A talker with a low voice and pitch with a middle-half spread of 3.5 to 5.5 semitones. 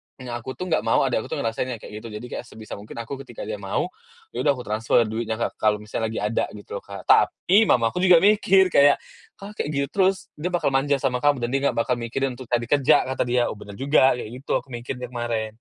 Yes: low, 125 Hz; average, 4.1 semitones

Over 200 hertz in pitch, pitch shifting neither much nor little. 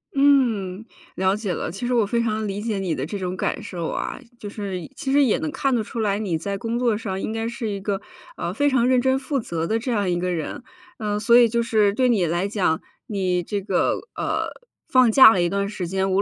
Yes: high, 210 Hz; average, 3.8 semitones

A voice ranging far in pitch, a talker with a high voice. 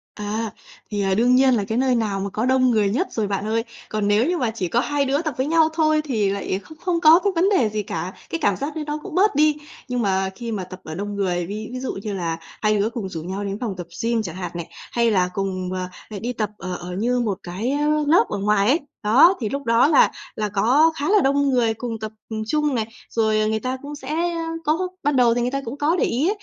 Yes: wide, 5.9 semitones; high, 230 Hz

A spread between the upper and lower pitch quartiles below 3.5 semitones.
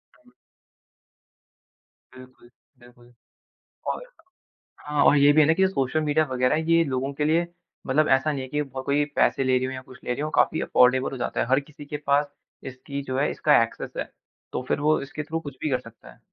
Yes: narrow, 2.6 semitones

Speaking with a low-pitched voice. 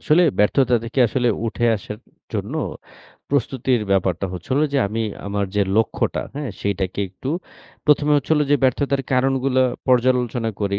Yes: low, 125 Hz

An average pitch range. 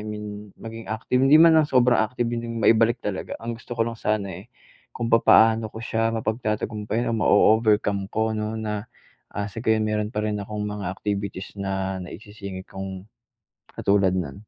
No: narrow, 1.8 semitones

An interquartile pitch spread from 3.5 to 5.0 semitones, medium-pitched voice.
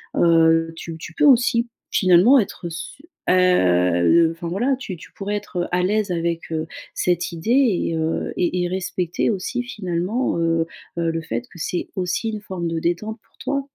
Yes: average, 4.0 semitones; medium, 175 Hz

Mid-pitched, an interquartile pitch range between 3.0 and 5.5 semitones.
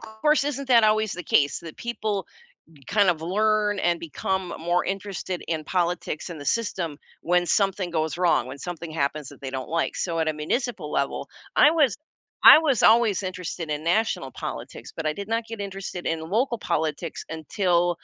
Yes: medium, 180 Hz; average, 4.9 semitones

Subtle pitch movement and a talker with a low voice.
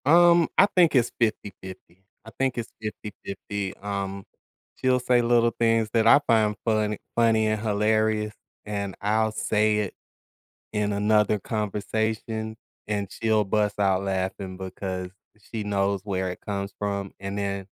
Yes: narrow, 2.1 semitones; low, 105 Hz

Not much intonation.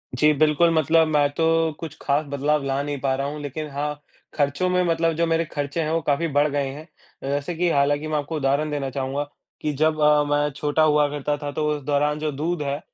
Yes: narrow, 1.6 semitones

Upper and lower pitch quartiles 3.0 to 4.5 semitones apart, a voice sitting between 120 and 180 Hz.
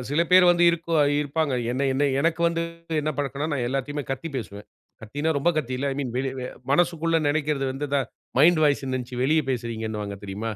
Yes: average, 3.7 semitones; medium, 140 Hz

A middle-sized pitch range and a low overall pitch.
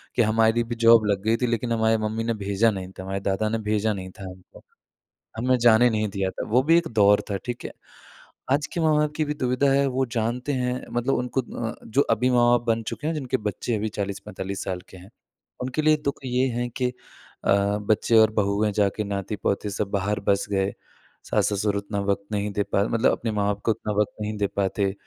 Yes: average, 3.4 semitones; low, 110 Hz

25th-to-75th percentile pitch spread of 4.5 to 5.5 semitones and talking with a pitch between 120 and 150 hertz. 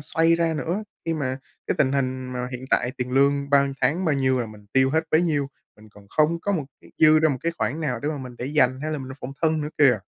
No: average, 3.5 semitones; medium, 140 Hz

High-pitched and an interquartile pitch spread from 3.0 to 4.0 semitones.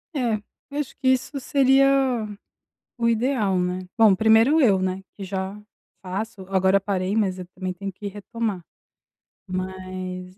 Yes: high, 195 Hz; average, 3.6 semitones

